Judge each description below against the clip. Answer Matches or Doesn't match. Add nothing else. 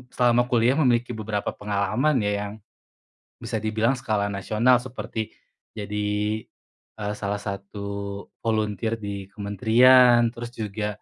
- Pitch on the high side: Doesn't match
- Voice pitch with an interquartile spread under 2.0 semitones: Doesn't match